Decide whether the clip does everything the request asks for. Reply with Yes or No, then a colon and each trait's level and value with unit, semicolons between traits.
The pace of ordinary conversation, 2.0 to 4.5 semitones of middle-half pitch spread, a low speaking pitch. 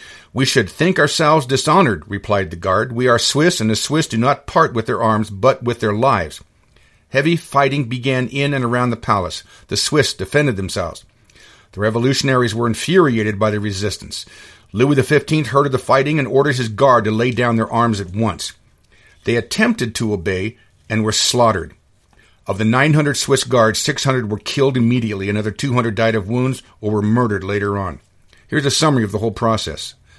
Yes: average, 195 wpm; average, 4.1 semitones; low, 120 Hz